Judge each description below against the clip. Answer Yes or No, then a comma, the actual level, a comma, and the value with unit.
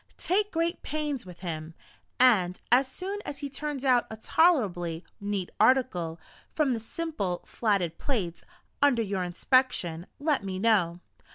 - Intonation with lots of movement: Yes, wide, 8.0 semitones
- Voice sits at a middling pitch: No, high, 230 Hz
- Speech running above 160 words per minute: No, average, 145 wpm